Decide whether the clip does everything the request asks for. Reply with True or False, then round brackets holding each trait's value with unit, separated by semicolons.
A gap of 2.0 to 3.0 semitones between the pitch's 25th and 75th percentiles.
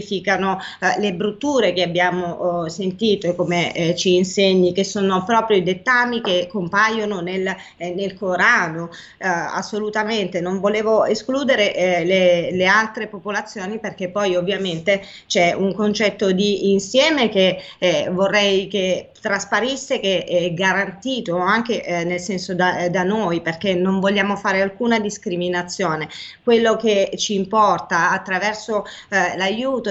True (2.6 semitones)